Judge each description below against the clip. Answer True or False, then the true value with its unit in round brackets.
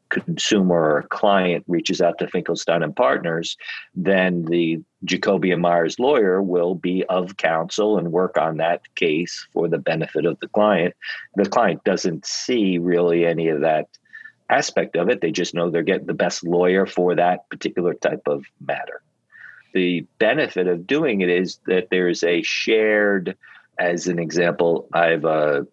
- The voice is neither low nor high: False (90 Hz)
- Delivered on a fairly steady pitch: True (1.4 semitones)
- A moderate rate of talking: True (165 wpm)